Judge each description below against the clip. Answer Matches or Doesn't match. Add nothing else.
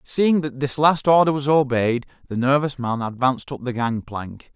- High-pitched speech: Doesn't match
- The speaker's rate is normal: Matches